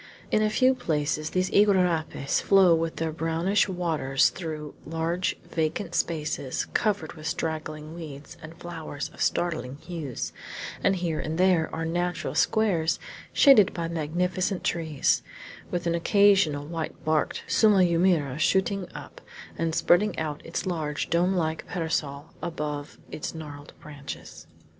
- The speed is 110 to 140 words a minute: Yes, slow, 135 wpm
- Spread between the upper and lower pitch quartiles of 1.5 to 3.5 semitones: Yes, average, 2.7 semitones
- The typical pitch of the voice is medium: Yes, medium, 165 Hz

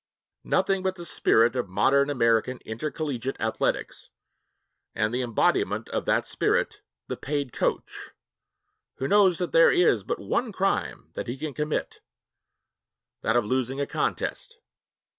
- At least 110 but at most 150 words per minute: Yes, average, 140 wpm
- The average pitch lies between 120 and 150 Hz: Yes, low, 135 Hz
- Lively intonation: Yes, wide, 6.0 semitones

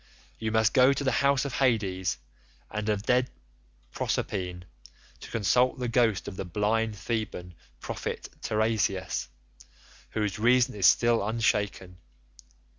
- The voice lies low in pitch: Yes, low, 110 Hz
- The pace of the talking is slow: Yes, slow, 125 wpm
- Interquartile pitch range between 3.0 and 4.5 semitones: Yes, average, 3.8 semitones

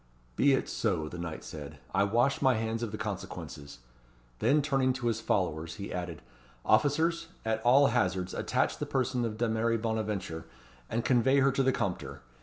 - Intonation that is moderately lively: No, wide, 6.3 semitones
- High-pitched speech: No, low, 110 Hz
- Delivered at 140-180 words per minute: Yes, average, 175 wpm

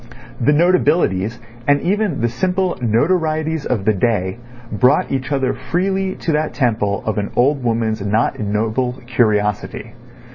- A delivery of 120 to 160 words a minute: Yes, average, 140 wpm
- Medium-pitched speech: No, low, 125 Hz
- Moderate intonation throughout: No, wide, 6.3 semitones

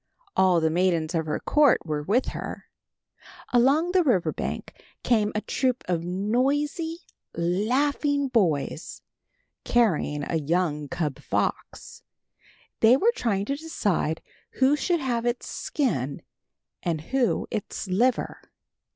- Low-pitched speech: No, high, 215 Hz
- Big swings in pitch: Yes, wide, 8.1 semitones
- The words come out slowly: Yes, slow, 125 wpm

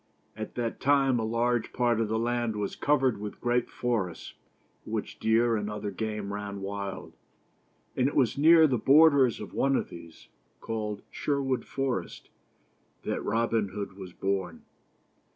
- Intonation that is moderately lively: Yes, average, 3.8 semitones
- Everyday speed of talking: Yes, average, 160 wpm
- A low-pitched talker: Yes, low, 115 Hz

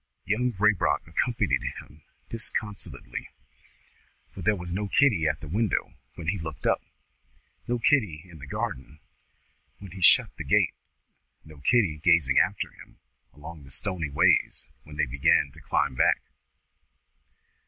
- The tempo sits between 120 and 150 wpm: Yes, average, 145 wpm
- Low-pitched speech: Yes, very low, 85 Hz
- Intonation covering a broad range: Yes, wide, 5.7 semitones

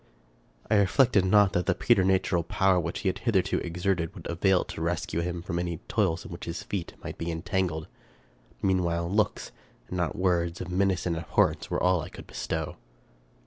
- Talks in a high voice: No, very low, 90 Hz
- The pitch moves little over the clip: Yes, narrow, 2.2 semitones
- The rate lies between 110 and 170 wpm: No, average, 185 wpm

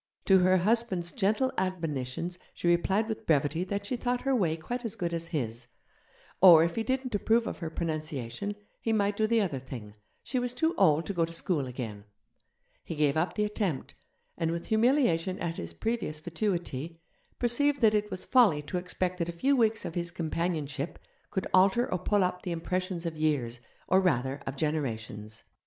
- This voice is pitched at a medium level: Yes, medium, 175 Hz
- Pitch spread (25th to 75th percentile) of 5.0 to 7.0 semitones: Yes, average, 5.3 semitones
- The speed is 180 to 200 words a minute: Yes, average, 190 wpm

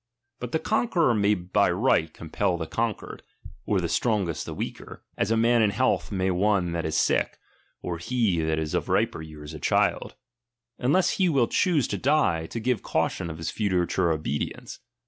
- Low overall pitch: Yes, low, 100 Hz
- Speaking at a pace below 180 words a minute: No, average, 190 wpm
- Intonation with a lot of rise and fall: Yes, wide, 6.3 semitones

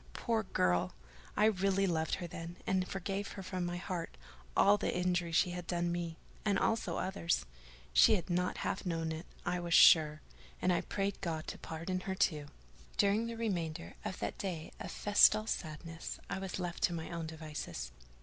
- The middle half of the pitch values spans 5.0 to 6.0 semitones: No, average, 2.7 semitones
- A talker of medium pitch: Yes, medium, 175 Hz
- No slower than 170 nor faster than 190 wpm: Yes, average, 180 wpm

